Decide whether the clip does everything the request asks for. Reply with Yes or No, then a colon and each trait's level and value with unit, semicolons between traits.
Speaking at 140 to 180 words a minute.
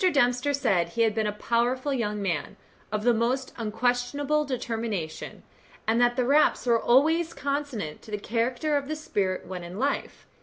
Yes: average, 175 wpm